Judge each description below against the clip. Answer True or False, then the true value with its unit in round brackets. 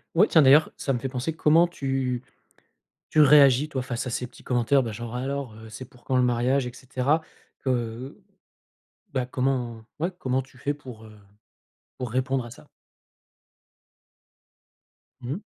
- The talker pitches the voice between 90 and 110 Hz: False (130 Hz)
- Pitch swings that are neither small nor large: False (2.3 semitones)